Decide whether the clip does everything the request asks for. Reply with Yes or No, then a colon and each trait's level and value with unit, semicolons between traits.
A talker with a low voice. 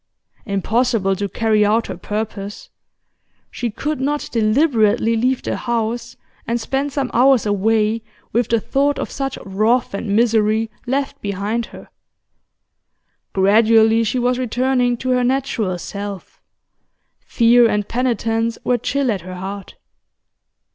No: high, 230 Hz